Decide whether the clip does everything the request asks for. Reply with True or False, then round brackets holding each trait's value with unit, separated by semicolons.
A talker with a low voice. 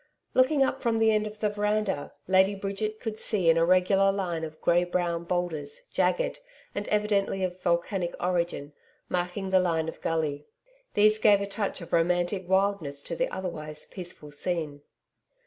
False (185 Hz)